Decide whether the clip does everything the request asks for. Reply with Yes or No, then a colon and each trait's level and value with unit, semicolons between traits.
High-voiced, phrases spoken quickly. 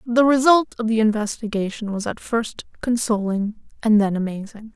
No: high, 220 Hz; average, 150 wpm